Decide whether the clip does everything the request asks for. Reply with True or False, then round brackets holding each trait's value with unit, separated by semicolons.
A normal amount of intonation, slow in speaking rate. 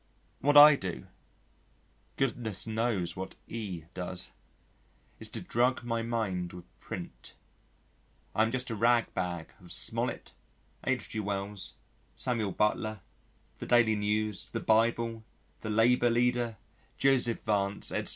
True (3.3 semitones; 125 wpm)